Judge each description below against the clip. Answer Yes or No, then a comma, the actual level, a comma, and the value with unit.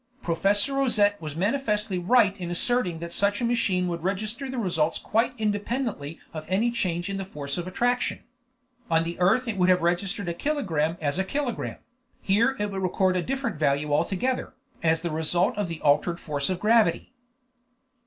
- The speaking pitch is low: No, high, 190 Hz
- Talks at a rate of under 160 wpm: No, average, 175 wpm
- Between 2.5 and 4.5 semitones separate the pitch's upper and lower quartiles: No, average, 5.1 semitones